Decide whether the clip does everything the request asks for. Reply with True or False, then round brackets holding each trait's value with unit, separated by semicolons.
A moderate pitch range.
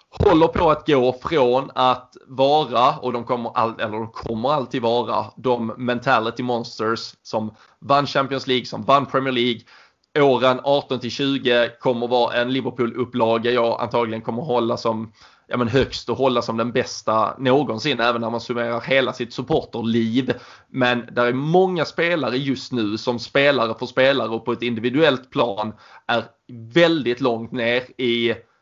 False (2.1 semitones)